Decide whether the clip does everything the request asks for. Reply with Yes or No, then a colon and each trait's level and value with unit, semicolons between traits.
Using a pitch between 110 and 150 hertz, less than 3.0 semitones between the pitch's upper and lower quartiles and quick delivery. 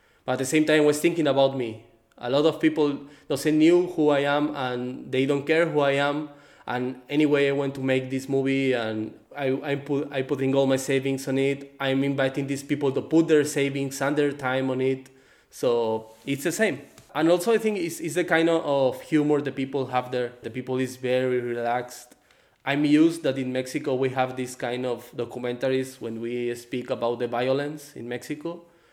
Yes: low, 135 Hz; narrow, 2.5 semitones; fast, 210 wpm